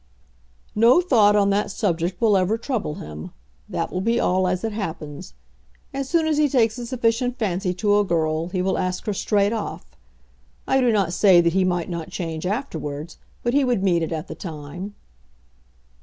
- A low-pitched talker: No, high, 195 Hz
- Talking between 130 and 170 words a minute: No, average, 190 wpm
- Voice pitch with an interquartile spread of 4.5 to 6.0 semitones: Yes, average, 4.8 semitones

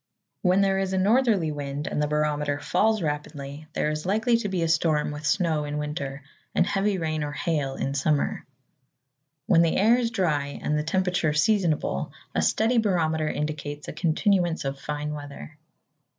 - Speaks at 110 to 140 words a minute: No, average, 175 wpm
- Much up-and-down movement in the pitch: No, average, 4.3 semitones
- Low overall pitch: No, medium, 155 Hz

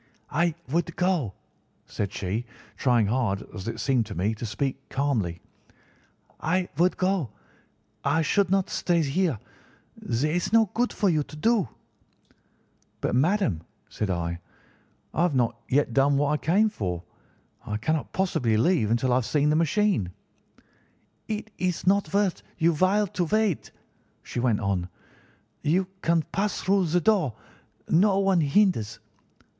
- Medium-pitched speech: Yes, medium, 150 Hz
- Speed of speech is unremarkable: Yes, average, 150 wpm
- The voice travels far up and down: Yes, wide, 8.3 semitones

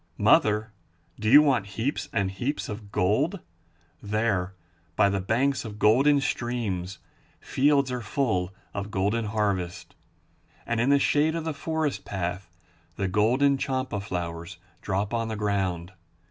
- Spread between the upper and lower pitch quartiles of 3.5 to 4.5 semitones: No, wide, 5.4 semitones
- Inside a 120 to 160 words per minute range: Yes, average, 140 wpm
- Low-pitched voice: Yes, low, 110 Hz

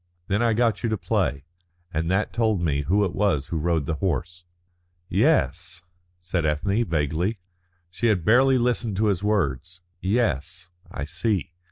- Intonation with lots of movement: No, average, 4.7 semitones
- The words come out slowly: No, average, 160 wpm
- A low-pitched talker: Yes, very low, 90 Hz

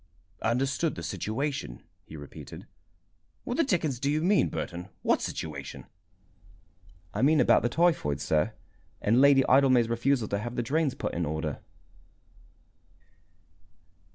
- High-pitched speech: No, low, 125 Hz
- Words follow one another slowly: Yes, slow, 130 wpm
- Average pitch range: No, wide, 8.4 semitones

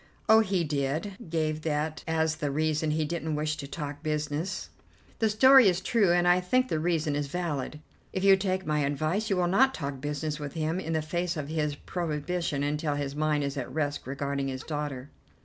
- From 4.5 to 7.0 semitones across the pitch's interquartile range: No, average, 3.3 semitones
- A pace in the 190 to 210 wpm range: Yes, average, 200 wpm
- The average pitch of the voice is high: No, medium, 155 Hz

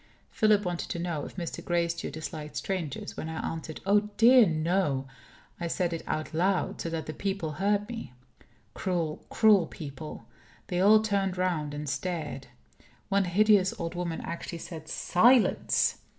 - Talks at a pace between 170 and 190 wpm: No, average, 155 wpm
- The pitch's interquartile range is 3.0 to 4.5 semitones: Yes, average, 3.8 semitones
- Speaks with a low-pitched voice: No, medium, 175 Hz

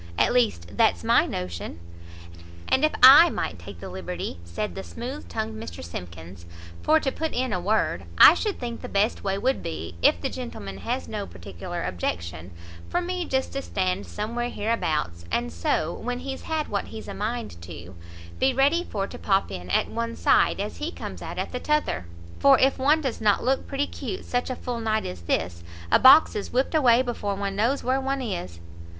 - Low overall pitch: No, high, 210 Hz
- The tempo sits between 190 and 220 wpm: Yes, average, 200 wpm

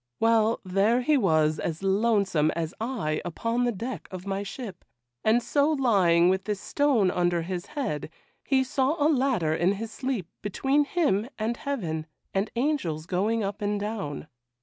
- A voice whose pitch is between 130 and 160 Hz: No, high, 205 Hz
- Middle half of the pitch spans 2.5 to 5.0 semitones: No, wide, 5.6 semitones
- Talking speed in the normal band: Yes, average, 165 wpm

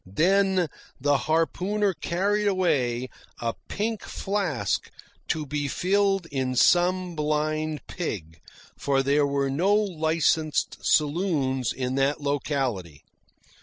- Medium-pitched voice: Yes, medium, 155 Hz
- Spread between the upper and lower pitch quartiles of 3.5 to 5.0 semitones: No, wide, 5.5 semitones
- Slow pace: Yes, slow, 105 wpm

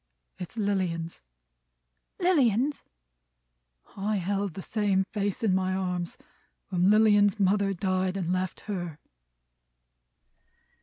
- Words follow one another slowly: Yes, slow, 100 wpm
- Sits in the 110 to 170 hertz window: No, high, 195 Hz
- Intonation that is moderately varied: No, narrow, 2.1 semitones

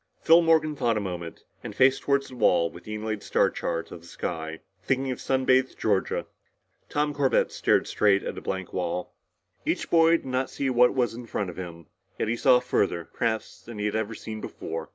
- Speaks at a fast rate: Yes, fast, 215 wpm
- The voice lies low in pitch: Yes, low, 110 Hz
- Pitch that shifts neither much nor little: No, wide, 6.0 semitones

